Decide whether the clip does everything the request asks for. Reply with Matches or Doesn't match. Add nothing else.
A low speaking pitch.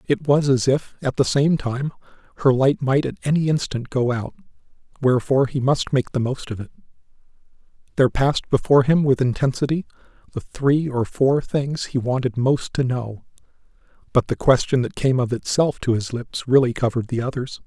Matches